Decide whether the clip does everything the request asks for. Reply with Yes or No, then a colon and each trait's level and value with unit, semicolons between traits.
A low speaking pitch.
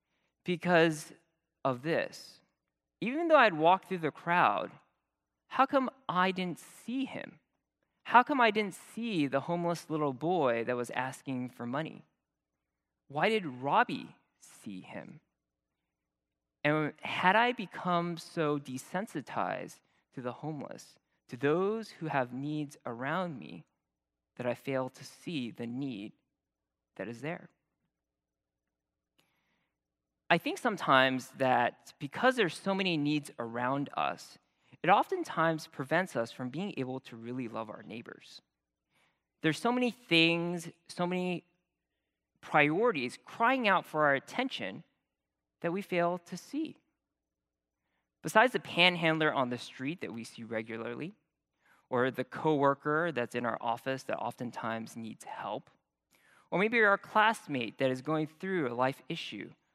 No: medium, 150 Hz